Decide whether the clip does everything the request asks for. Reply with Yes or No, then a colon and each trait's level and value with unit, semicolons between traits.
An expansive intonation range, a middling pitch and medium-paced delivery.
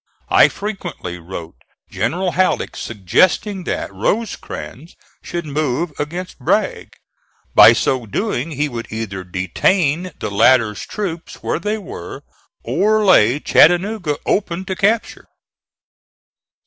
No: wide, 8.4 semitones; medium, 160 Hz; slow, 110 wpm